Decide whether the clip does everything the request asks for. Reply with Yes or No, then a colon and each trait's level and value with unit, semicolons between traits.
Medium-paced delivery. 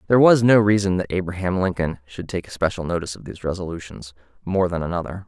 Yes: average, 195 wpm